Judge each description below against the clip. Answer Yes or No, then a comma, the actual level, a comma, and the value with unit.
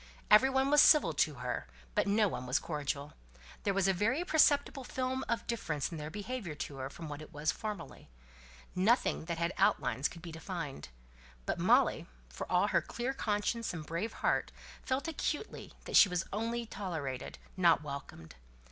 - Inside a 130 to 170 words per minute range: No, average, 185 wpm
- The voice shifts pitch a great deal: Yes, wide, 7.7 semitones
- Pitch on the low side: No, medium, 185 Hz